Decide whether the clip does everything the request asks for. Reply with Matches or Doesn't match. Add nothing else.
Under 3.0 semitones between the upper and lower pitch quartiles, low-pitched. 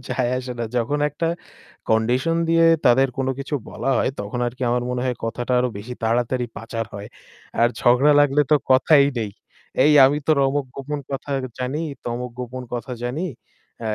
Matches